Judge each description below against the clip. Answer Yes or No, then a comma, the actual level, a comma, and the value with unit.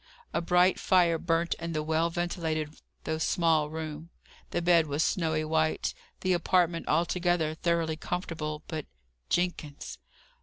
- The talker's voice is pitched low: No, medium, 165 Hz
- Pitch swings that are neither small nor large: No, narrow, 1.8 semitones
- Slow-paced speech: Yes, slow, 130 wpm